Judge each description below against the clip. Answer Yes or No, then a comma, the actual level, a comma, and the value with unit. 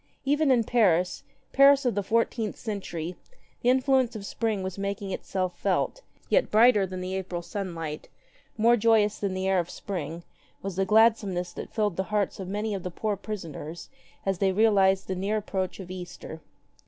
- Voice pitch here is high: Yes, high, 195 Hz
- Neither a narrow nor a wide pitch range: Yes, average, 3.1 semitones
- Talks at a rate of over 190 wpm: No, average, 180 wpm